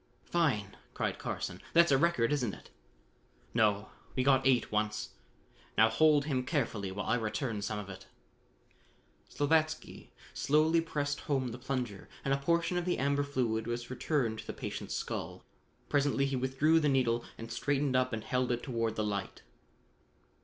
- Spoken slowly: No, average, 165 wpm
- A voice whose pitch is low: Yes, low, 130 Hz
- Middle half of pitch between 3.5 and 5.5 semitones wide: Yes, average, 4.4 semitones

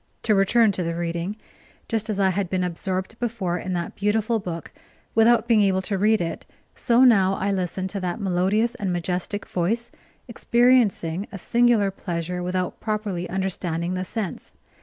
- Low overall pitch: No, high, 195 Hz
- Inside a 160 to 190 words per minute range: Yes, average, 165 wpm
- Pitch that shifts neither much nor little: Yes, average, 3.5 semitones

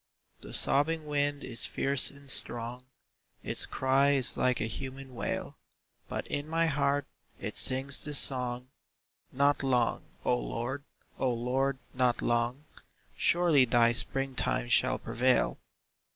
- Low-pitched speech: Yes, low, 130 Hz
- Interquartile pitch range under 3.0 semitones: Yes, narrow, 2.5 semitones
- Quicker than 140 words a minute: No, slow, 135 wpm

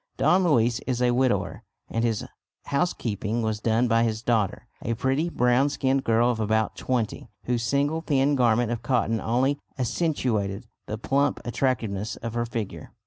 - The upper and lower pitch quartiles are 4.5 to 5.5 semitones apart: No, average, 3.0 semitones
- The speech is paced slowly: No, average, 160 wpm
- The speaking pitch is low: Yes, low, 120 Hz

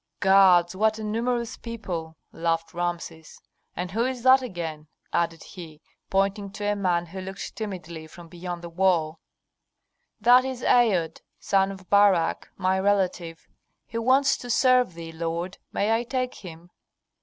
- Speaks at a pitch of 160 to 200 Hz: Yes, high, 190 Hz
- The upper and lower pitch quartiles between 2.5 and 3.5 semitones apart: No, average, 4.5 semitones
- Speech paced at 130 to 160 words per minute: Yes, average, 150 wpm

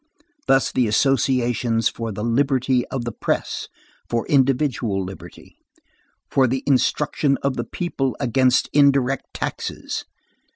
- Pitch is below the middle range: Yes, low, 130 Hz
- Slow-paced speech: Yes, slow, 120 wpm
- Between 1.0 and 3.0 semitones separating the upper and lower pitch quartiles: Yes, narrow, 2.5 semitones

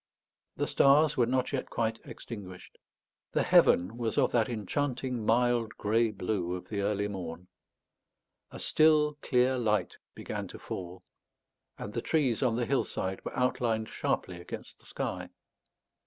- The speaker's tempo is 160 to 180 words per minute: No, average, 145 wpm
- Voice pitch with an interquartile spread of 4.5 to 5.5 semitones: No, average, 3.8 semitones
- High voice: No, low, 115 Hz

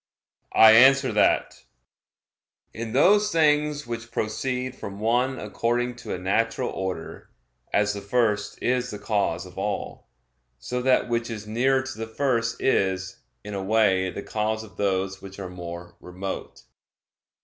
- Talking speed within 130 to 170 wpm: Yes, average, 150 wpm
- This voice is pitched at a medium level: No, low, 110 Hz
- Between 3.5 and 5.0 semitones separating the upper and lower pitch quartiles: Yes, average, 4.3 semitones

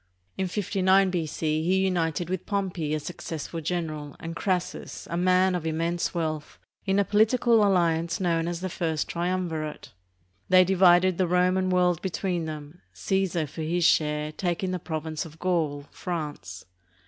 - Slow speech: No, average, 150 wpm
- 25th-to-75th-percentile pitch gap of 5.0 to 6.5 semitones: No, narrow, 2.6 semitones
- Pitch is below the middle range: No, medium, 175 Hz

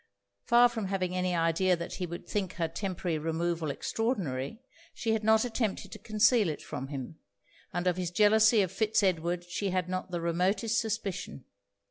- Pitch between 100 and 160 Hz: No, medium, 185 Hz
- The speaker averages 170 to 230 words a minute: Yes, average, 175 wpm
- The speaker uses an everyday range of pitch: Yes, average, 4.1 semitones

